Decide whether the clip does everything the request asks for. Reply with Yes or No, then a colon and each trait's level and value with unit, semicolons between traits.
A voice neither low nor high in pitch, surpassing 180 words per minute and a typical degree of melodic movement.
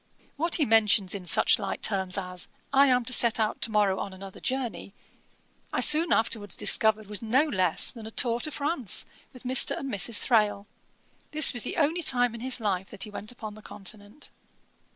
No: high, 220 Hz; average, 195 wpm; average, 4.1 semitones